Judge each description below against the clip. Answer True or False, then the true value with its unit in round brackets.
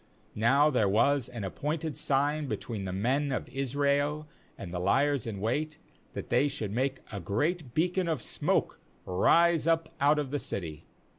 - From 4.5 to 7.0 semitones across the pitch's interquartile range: True (5.1 semitones)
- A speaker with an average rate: True (165 wpm)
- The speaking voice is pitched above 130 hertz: True (140 Hz)